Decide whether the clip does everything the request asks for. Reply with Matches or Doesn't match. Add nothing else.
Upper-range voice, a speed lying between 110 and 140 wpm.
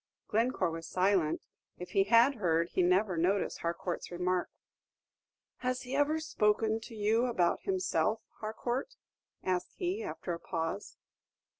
Matches